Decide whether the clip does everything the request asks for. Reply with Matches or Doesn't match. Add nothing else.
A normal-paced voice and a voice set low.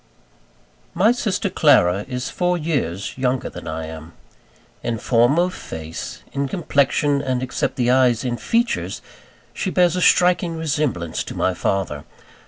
Matches